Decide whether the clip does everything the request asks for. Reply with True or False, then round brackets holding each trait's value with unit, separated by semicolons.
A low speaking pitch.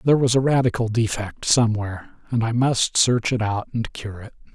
True (115 Hz)